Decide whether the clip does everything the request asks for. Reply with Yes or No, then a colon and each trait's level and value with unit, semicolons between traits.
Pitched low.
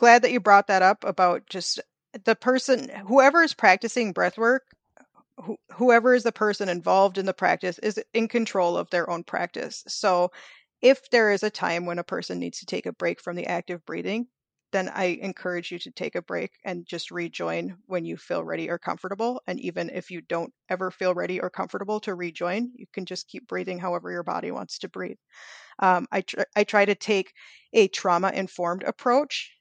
No: high, 195 Hz